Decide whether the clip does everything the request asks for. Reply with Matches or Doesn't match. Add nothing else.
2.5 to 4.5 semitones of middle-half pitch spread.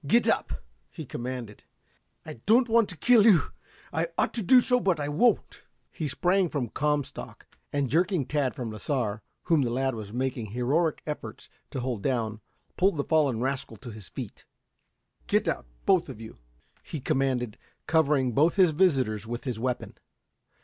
Doesn't match